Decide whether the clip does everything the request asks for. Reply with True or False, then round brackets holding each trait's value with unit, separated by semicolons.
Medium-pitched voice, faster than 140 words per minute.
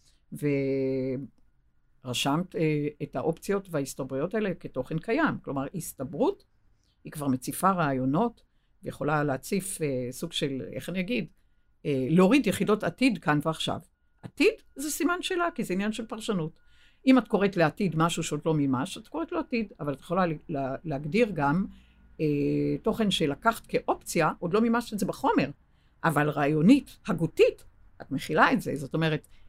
True (160 Hz; 150 wpm)